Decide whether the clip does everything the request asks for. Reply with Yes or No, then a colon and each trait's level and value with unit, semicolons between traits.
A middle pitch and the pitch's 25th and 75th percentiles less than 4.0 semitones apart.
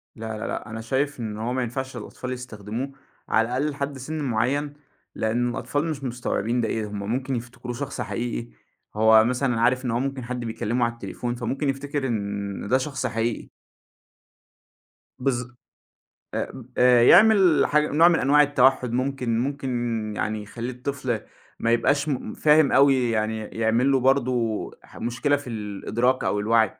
No: low, 125 Hz; average, 3.2 semitones